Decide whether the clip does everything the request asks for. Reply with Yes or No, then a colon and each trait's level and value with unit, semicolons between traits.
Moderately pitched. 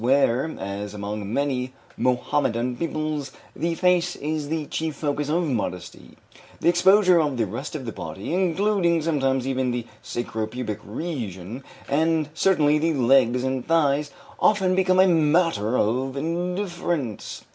Yes: medium, 145 Hz